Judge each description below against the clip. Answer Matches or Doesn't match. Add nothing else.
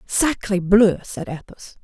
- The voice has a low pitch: Doesn't match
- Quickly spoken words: Doesn't match